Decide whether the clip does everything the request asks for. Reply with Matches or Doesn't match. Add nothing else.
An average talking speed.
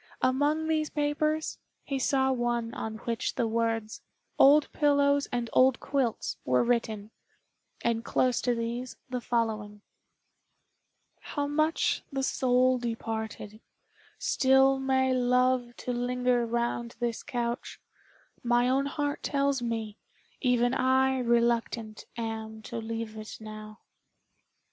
Doesn't match